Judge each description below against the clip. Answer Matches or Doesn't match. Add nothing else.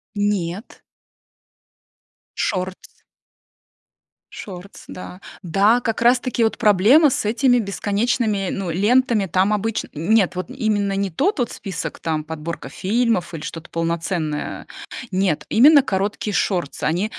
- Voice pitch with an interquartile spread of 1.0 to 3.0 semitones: Doesn't match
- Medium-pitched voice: Doesn't match